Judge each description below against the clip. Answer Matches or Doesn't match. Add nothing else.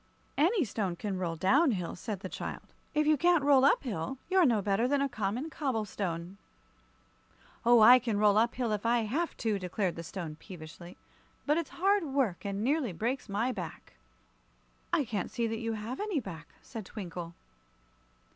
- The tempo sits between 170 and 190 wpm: Matches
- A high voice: Matches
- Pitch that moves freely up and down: Matches